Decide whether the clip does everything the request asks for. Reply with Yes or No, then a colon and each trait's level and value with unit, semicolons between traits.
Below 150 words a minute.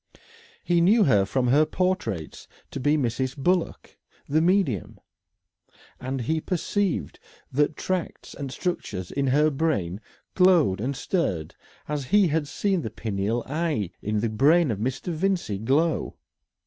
Yes: average, 140 wpm